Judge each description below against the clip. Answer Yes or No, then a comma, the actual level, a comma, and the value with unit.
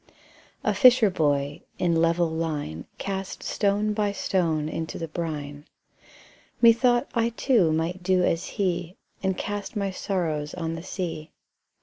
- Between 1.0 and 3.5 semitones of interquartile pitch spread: No, average, 4.0 semitones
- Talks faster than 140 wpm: No, slow, 135 wpm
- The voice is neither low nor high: Yes, medium, 175 Hz